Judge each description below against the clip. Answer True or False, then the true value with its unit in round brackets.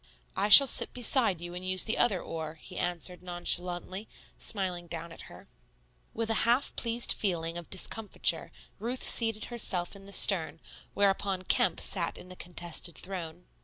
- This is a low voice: False (185 Hz)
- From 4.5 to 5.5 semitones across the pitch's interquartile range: False (3.4 semitones)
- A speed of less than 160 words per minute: False (165 wpm)